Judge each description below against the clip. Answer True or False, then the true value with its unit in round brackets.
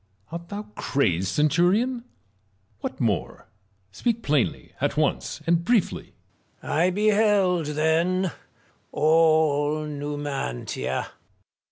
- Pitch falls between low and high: True (160 Hz)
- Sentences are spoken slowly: True (95 wpm)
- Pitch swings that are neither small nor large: True (4.1 semitones)